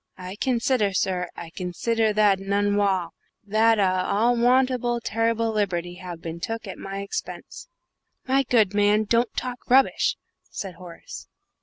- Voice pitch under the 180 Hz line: No, high, 205 Hz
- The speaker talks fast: No, average, 145 wpm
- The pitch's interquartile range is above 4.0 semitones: No, average, 3.7 semitones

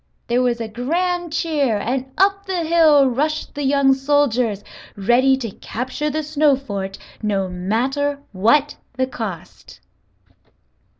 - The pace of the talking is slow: Yes, slow, 130 wpm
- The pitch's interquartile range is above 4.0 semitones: Yes, average, 4.6 semitones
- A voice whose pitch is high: Yes, very high, 270 Hz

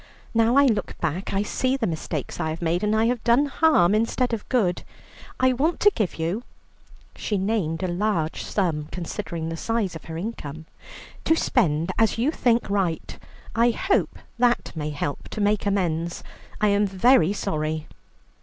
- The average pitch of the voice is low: No, high, 200 Hz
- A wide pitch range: Yes, wide, 6.0 semitones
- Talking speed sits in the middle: Yes, average, 175 wpm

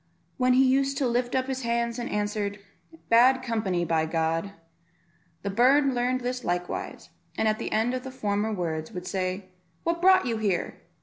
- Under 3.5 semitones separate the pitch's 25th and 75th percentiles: No, wide, 5.5 semitones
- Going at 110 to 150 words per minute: No, average, 185 wpm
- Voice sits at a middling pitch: No, high, 230 Hz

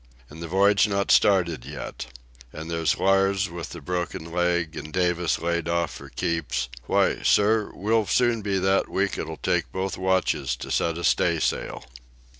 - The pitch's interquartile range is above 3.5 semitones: No, average, 2.9 semitones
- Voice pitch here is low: Yes, very low, 90 Hz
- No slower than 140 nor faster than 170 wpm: Yes, average, 160 wpm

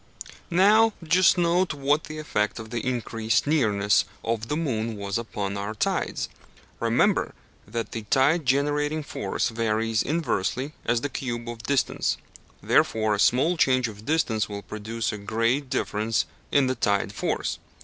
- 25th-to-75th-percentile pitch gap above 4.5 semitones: Yes, average, 5.2 semitones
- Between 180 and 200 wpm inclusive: No, average, 150 wpm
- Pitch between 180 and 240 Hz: No, low, 120 Hz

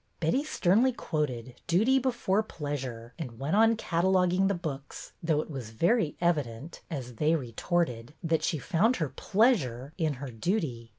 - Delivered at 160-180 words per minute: Yes, average, 175 wpm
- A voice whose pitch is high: No, medium, 160 Hz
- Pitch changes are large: Yes, wide, 6.3 semitones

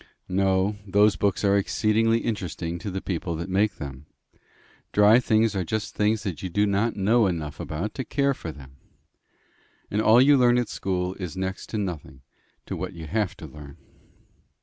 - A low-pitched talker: Yes, low, 100 Hz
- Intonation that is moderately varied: Yes, average, 4.0 semitones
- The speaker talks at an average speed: Yes, average, 180 wpm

